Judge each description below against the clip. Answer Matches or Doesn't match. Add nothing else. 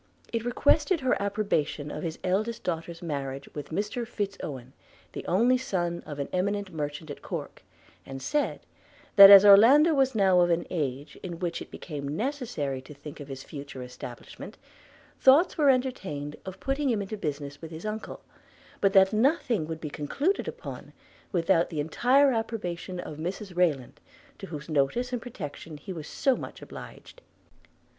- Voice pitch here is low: Doesn't match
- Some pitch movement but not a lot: Doesn't match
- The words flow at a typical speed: Matches